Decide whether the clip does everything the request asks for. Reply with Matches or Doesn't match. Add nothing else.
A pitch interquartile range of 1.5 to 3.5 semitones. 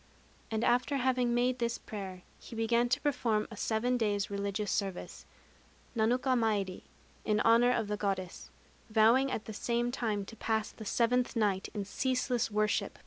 Matches